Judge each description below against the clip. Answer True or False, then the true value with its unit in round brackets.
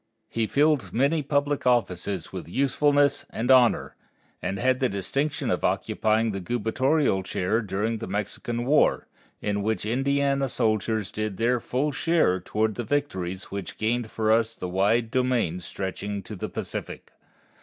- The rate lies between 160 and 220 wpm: False (150 wpm)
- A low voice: True (115 Hz)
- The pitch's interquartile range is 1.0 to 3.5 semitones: False (4.7 semitones)